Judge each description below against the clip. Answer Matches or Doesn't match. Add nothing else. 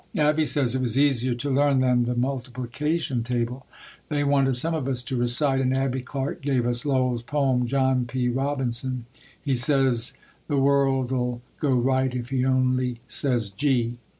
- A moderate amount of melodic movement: Doesn't match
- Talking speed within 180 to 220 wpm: Doesn't match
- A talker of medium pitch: Doesn't match